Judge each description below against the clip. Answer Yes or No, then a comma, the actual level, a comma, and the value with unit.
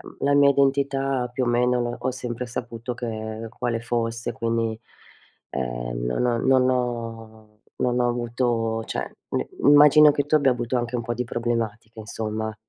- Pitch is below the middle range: Yes, low, 120 Hz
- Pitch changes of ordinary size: No, narrow, 1.9 semitones